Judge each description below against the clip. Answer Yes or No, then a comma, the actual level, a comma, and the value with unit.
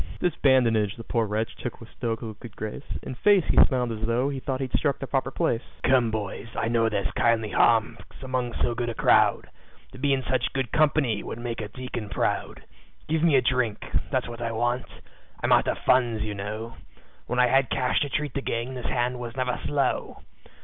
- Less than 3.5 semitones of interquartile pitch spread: Yes, narrow, 2.6 semitones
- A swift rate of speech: Yes, fast, 210 wpm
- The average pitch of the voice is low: Yes, low, 120 Hz